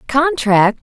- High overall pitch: Yes, very high, 250 Hz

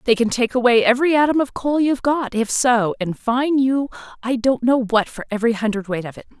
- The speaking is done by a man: No, female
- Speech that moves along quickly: Yes, fast, 225 wpm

